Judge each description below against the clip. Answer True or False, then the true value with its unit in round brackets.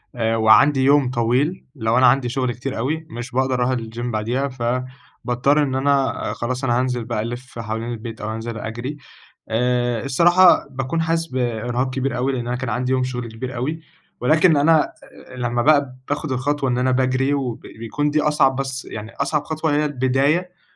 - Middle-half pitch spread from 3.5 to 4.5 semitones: False (2.8 semitones)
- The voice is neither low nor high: False (130 Hz)